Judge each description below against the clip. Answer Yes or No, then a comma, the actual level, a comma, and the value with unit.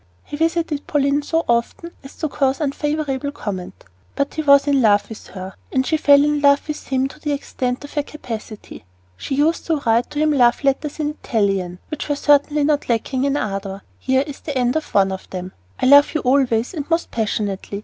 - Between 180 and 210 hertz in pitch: No, very high, 280 Hz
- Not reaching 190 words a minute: No, fast, 205 wpm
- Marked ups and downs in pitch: No, average, 4.4 semitones